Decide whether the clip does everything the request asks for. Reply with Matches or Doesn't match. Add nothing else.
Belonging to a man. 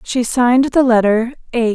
Doesn't match